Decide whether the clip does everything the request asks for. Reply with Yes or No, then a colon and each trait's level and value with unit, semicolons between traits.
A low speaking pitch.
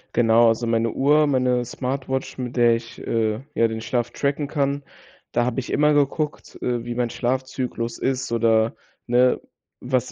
Yes: low, 125 Hz